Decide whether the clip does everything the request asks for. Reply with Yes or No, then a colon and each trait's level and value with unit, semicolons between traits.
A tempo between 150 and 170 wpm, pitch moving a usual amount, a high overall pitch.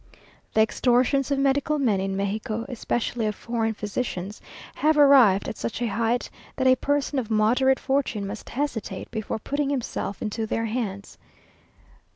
Yes: average, 155 wpm; average, 3.9 semitones; high, 235 Hz